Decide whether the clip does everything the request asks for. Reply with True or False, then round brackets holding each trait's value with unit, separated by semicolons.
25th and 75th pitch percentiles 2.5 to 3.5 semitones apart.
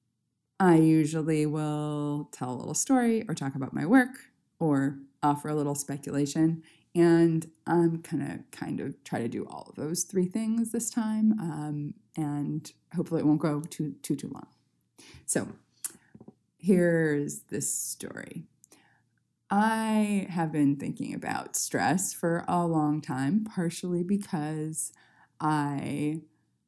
True (3.2 semitones)